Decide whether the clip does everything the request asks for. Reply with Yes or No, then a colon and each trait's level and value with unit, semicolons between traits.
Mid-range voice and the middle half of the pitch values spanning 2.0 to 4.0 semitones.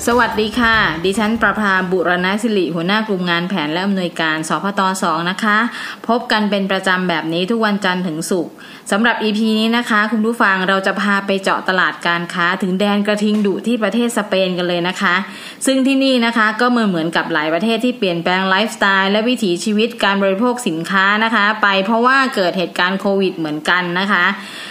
No: high, 200 Hz; average, 3.4 semitones